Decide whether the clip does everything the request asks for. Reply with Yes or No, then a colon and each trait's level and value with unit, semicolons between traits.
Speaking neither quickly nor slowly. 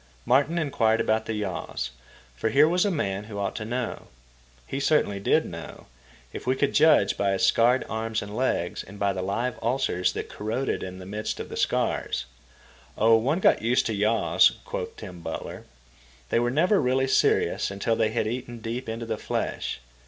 Yes: average, 185 wpm